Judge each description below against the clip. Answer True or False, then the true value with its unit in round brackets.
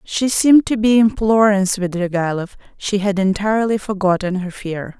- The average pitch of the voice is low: False (200 Hz)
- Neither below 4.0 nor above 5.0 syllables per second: True (4.9 syllables/s)